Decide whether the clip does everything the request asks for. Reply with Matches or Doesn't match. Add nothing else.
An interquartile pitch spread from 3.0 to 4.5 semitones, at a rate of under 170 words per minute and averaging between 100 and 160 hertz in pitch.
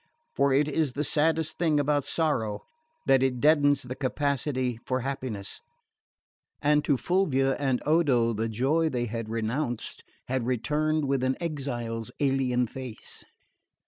Matches